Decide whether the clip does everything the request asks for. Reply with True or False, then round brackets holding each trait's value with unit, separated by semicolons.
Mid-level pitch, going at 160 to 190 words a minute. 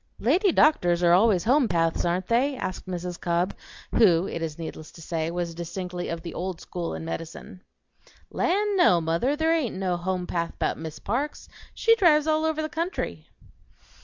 True (180 Hz; 170 wpm)